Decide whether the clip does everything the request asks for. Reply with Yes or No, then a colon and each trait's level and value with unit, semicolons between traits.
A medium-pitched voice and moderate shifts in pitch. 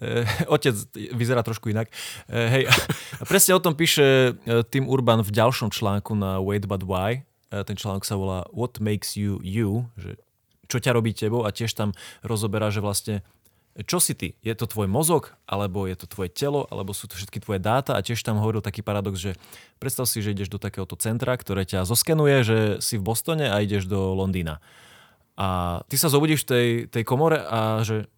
No: low, 110 Hz; average, 3.5 semitones